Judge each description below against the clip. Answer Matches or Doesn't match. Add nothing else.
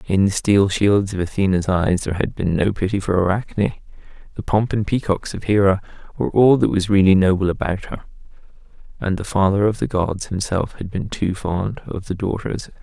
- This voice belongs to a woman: Doesn't match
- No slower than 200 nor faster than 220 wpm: Matches